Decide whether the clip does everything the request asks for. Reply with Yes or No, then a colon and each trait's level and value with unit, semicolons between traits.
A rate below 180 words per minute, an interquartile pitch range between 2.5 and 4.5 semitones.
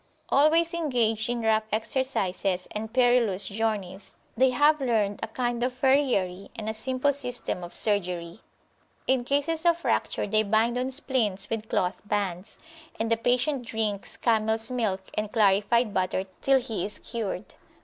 Yes: average, 150 wpm; average, 3.8 semitones